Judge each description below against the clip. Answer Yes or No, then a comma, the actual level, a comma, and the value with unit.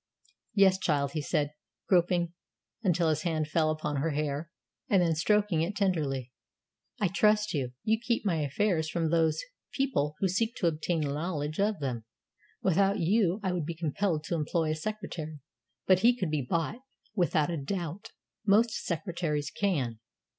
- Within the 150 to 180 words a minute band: Yes, average, 160 wpm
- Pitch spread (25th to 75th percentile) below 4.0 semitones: No, average, 4.4 semitones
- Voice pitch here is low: No, medium, 170 Hz